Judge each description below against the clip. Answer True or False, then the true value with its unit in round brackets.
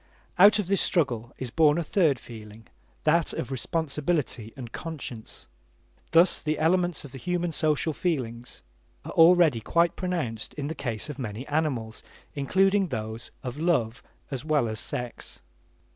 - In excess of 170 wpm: False (150 wpm)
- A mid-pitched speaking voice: True (150 Hz)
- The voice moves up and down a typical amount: False (6.0 semitones)